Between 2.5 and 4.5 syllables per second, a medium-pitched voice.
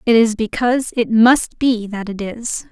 No: 4.3 syllables/s; high, 230 Hz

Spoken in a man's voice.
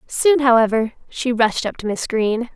No: female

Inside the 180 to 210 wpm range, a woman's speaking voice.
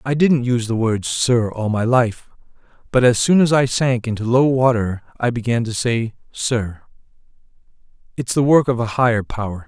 No: average, 185 wpm; male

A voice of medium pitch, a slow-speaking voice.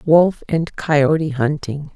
Yes: medium, 155 Hz; slow, 125 wpm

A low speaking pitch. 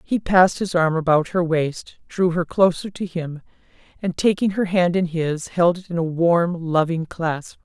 No: medium, 170 Hz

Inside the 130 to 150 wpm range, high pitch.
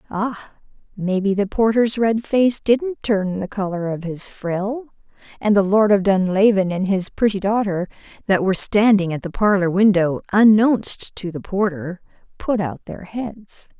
No: average, 160 wpm; high, 200 Hz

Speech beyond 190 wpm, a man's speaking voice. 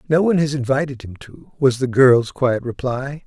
Yes: average, 200 wpm; male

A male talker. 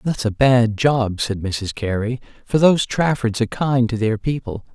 Yes: male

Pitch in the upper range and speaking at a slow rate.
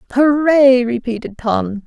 Yes: very high, 250 Hz; slow, 95 wpm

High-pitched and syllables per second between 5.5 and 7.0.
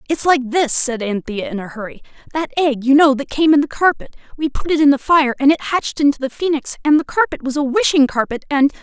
Yes: very high, 285 Hz; 5.9 syllables/s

